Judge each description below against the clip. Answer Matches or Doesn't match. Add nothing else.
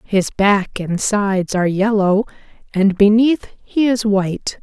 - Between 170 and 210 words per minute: Doesn't match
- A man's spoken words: Doesn't match